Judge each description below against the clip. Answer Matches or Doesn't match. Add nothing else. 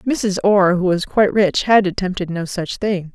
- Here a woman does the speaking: Matches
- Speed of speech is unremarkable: Doesn't match